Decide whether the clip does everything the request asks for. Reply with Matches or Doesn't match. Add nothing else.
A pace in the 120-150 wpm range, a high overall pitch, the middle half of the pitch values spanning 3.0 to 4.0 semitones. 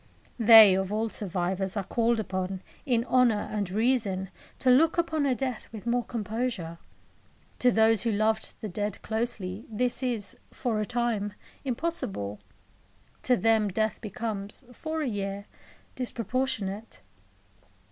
Matches